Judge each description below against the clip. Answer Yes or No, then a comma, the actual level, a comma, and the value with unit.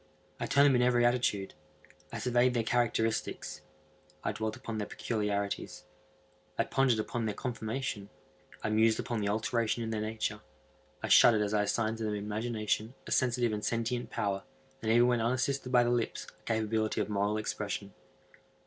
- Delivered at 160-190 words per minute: Yes, average, 175 wpm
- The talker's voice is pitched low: Yes, low, 110 Hz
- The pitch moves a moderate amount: No, narrow, 2.2 semitones